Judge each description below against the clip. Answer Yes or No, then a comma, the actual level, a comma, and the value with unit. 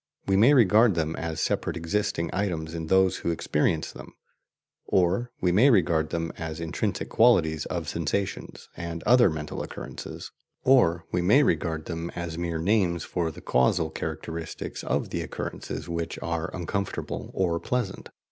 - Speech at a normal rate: Yes, average, 155 wpm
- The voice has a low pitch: Yes, very low, 85 Hz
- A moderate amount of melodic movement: Yes, average, 3.3 semitones